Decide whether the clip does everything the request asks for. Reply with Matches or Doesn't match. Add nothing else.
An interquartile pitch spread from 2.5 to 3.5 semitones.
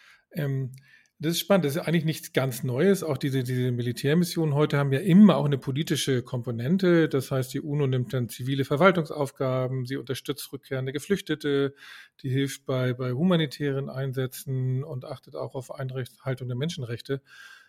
Matches